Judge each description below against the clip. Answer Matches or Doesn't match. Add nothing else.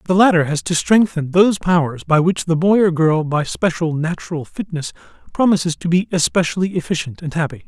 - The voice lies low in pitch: Doesn't match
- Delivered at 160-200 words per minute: Matches